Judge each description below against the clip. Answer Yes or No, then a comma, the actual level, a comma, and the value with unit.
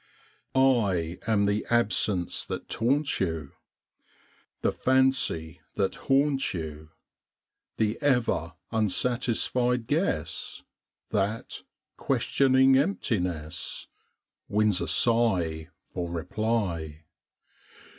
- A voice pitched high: No, low, 110 Hz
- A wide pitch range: Yes, wide, 6.7 semitones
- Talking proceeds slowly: Yes, slow, 80 wpm